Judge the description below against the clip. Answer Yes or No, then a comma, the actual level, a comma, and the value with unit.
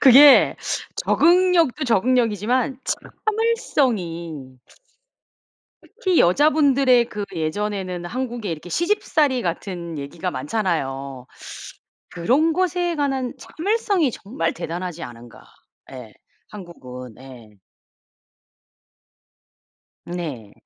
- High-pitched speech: Yes, high, 210 Hz